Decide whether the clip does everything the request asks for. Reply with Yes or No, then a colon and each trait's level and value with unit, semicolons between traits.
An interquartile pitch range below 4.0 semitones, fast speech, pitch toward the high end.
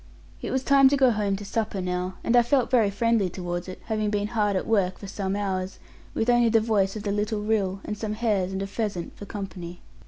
Yes: average, 2.8 semitones; fast, 240 wpm; high, 205 Hz